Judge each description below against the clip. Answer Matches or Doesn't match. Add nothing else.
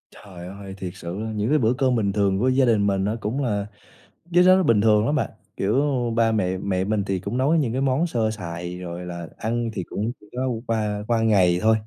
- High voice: Doesn't match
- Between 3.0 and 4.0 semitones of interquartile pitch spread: Matches